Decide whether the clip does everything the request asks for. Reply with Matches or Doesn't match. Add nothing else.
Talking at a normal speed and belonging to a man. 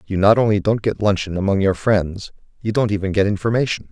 Doesn't match